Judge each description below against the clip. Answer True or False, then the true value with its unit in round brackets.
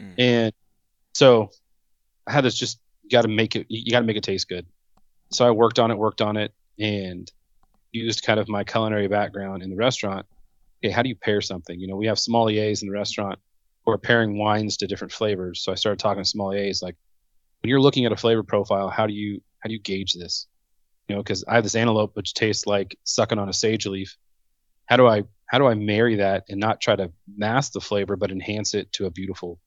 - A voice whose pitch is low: True (105 Hz)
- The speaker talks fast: True (230 wpm)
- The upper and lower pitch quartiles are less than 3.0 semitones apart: True (2.6 semitones)